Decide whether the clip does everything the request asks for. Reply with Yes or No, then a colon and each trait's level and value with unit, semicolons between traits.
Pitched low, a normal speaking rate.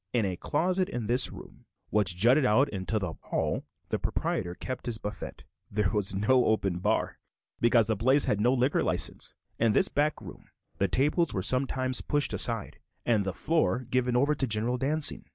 Yes: low, 120 Hz; average, 185 wpm